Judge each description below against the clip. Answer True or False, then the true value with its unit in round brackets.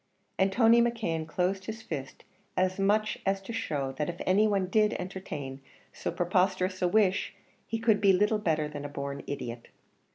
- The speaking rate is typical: True (175 wpm)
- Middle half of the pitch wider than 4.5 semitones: True (5.1 semitones)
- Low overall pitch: False (185 Hz)